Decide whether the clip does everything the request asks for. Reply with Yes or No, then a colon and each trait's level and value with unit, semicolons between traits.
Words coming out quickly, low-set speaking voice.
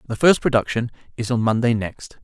No: average, 190 wpm; low, 115 Hz